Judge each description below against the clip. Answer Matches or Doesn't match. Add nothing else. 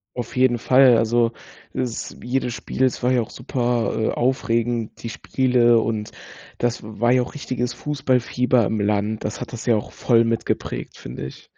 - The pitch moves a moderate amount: Doesn't match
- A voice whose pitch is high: Doesn't match